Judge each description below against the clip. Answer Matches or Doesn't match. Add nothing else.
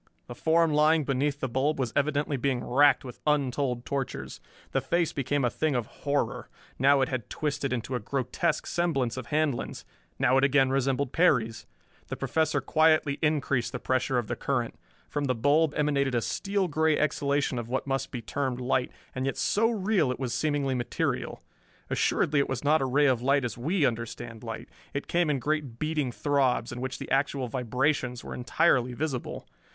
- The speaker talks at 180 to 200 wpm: Matches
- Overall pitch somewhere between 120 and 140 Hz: Matches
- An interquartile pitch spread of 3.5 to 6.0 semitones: Doesn't match